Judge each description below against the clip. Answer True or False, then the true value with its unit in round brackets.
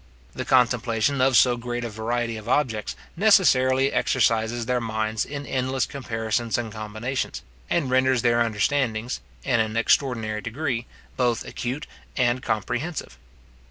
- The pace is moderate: False (130 wpm)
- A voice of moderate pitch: False (120 Hz)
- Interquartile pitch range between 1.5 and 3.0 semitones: True (2.6 semitones)